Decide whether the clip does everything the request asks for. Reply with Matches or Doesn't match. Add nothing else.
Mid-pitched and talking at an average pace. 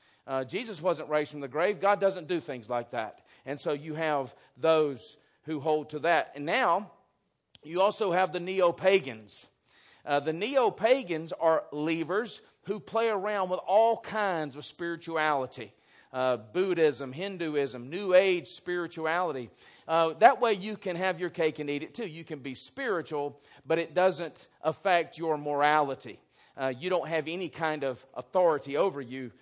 Matches